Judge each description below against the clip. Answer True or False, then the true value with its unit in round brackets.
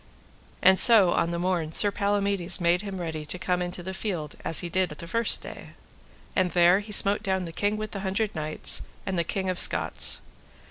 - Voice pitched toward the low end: False (185 Hz)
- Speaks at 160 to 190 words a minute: False (205 wpm)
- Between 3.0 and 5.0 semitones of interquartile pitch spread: False (2.6 semitones)